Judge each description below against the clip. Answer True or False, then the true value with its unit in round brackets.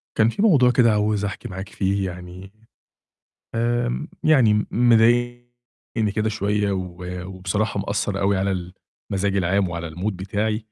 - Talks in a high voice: False (105 Hz)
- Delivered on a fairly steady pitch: False (3.4 semitones)